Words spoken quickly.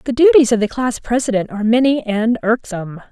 No: average, 195 wpm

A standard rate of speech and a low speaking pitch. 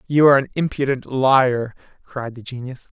Yes: average, 160 wpm; low, 130 Hz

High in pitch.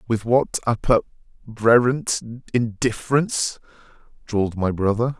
No: low, 115 Hz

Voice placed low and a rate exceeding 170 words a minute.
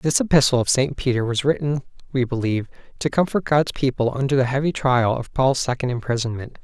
Yes: low, 130 Hz; average, 190 wpm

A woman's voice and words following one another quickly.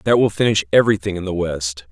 No: male; fast, 220 wpm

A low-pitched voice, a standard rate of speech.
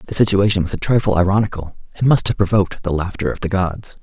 No: very low, 95 Hz; fast, 225 wpm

